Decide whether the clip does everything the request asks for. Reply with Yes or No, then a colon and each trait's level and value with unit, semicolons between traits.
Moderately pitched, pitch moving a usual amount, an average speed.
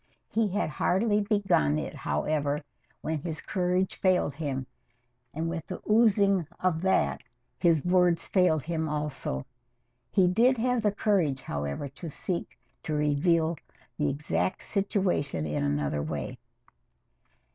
No: medium, 165 Hz; average, 5.0 semitones; slow, 130 wpm